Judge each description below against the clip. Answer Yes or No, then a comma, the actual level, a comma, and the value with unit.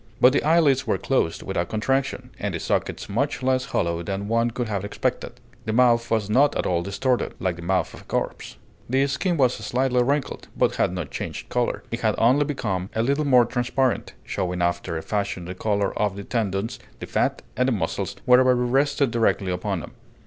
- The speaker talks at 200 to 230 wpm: Yes, fast, 205 wpm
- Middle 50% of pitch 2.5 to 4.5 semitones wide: No, average, 4.9 semitones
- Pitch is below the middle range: Yes, low, 115 Hz